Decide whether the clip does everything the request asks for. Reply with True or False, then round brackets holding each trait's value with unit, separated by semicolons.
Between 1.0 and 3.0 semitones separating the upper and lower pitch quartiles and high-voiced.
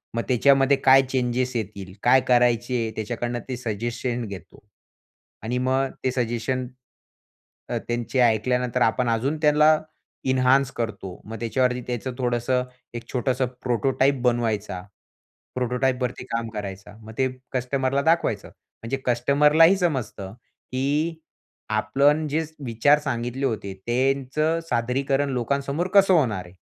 False (2.7 semitones; 125 Hz)